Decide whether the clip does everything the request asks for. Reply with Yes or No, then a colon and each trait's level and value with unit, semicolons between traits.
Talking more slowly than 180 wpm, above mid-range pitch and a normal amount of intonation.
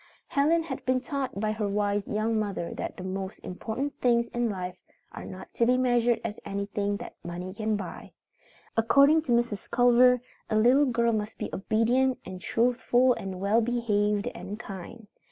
Yes: average, 170 wpm; high, 225 Hz; average, 3.4 semitones